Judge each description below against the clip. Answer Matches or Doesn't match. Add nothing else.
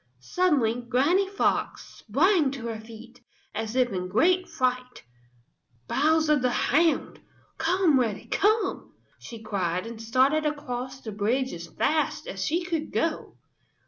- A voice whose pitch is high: Matches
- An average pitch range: Doesn't match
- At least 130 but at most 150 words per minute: Matches